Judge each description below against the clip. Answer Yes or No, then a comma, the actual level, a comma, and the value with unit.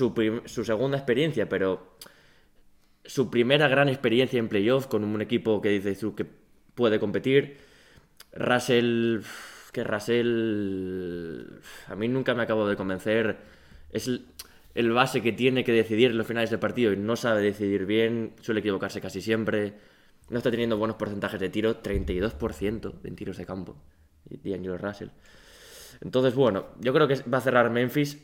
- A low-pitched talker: Yes, low, 110 Hz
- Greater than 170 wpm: No, average, 155 wpm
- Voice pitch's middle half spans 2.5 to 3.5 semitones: Yes, average, 3.2 semitones